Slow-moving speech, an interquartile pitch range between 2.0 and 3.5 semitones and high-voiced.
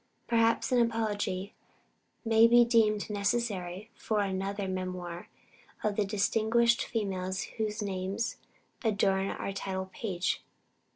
Yes: slow, 110 wpm; average, 3.0 semitones; high, 205 Hz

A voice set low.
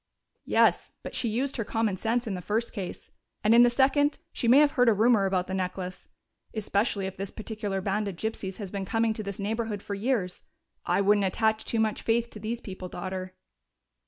No: high, 215 Hz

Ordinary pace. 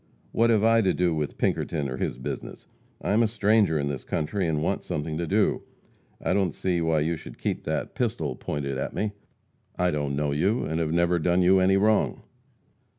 No: fast, 210 wpm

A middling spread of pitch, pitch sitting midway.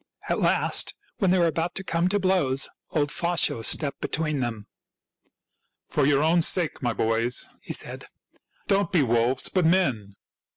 No: wide, 6.1 semitones; medium, 155 Hz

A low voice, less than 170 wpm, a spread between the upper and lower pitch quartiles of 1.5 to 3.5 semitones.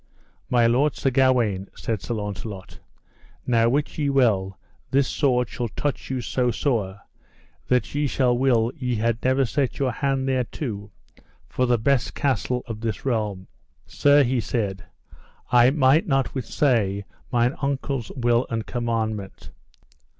Yes: low, 120 Hz; average, 145 wpm; average, 3.2 semitones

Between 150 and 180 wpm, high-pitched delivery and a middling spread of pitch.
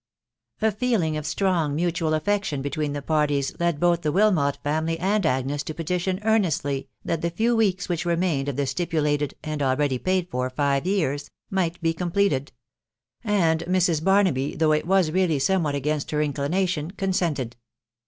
No: average, 165 wpm; medium, 160 Hz; average, 4.2 semitones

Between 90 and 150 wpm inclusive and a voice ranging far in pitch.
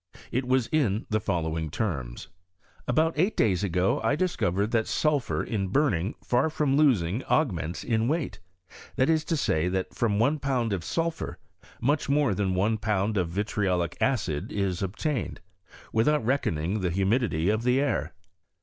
No: average, 160 wpm; wide, 6.7 semitones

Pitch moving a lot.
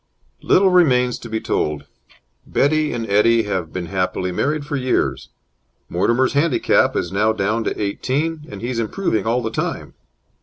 Yes: wide, 6.1 semitones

